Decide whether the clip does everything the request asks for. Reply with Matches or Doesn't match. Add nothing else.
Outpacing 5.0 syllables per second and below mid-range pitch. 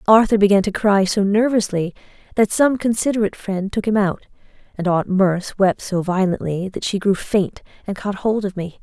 Doesn't match